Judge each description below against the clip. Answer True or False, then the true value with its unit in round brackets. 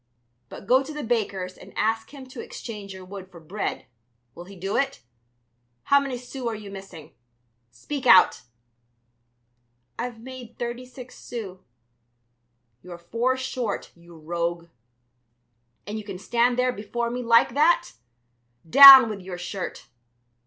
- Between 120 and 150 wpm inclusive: True (145 wpm)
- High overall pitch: True (225 Hz)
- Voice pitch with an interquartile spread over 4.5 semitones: True (5.0 semitones)